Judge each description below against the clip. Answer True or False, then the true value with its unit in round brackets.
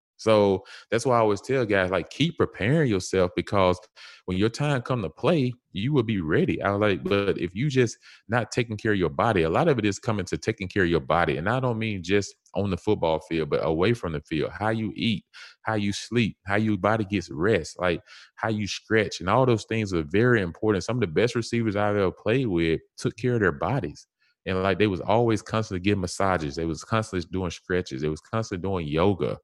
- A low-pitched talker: True (105 Hz)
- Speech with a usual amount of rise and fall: True (3.4 semitones)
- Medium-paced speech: False (235 wpm)